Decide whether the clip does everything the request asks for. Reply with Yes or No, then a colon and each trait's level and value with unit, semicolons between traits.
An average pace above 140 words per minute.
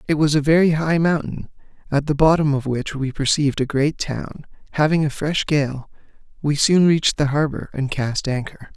Yes: average, 190 wpm